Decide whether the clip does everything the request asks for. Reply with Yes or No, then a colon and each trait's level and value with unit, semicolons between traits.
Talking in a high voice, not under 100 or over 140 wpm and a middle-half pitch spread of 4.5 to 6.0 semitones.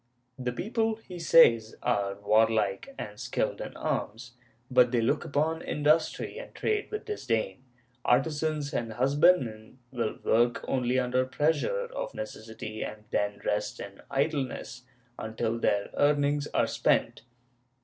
No: low, 125 Hz; slow, 135 wpm; wide, 5.6 semitones